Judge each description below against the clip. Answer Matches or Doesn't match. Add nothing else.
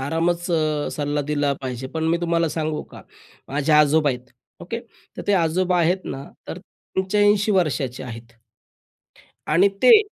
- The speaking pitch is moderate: Matches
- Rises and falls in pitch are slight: Doesn't match